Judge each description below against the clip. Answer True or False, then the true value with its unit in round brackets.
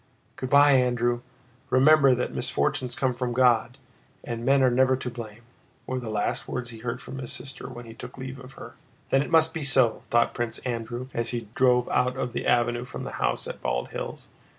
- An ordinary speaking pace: False (210 wpm)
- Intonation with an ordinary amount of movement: False (1.7 semitones)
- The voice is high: False (125 Hz)